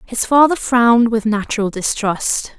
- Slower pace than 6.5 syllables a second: Yes, 4.5 syllables/s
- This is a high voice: Yes, high, 230 Hz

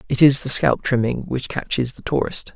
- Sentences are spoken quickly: Yes, fast, 210 wpm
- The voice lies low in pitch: Yes, low, 130 Hz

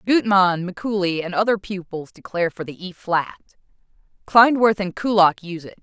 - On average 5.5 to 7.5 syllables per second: No, 5.0 syllables/s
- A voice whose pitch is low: No, high, 190 Hz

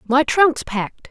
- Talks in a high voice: Yes, very high, 270 Hz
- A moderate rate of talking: Yes, average, 165 wpm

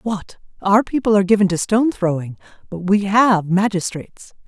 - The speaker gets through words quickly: No, average, 160 wpm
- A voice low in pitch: No, high, 200 Hz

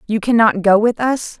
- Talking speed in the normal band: No, fast, 215 wpm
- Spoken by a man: No, female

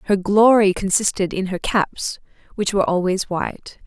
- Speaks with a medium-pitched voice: No, high, 195 Hz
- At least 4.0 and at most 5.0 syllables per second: Yes, 4.9 syllables/s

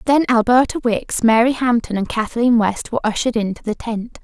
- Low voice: No, high, 230 Hz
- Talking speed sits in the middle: Yes, average, 185 wpm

